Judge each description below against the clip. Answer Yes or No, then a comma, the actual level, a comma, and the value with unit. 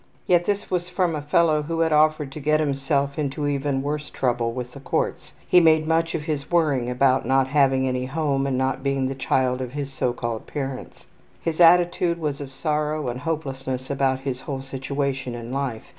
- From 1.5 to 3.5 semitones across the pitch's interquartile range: Yes, average, 2.8 semitones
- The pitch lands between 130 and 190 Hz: Yes, medium, 140 Hz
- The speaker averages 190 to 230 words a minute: Yes, average, 200 wpm